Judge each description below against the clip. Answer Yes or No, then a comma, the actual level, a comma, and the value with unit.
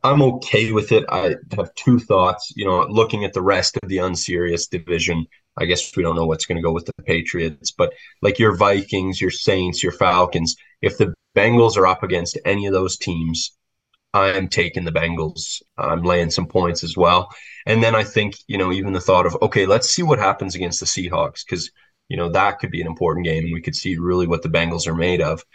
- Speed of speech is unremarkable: No, fast, 225 wpm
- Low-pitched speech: Yes, very low, 90 Hz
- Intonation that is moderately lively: Yes, average, 3.1 semitones